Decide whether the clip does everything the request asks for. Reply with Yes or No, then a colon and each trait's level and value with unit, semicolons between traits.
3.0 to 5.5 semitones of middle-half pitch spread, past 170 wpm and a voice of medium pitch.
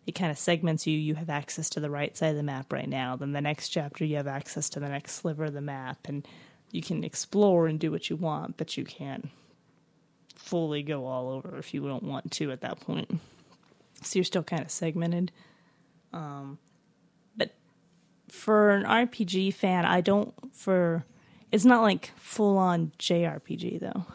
Yes: average, 4.2 semitones; average, 190 wpm; medium, 165 Hz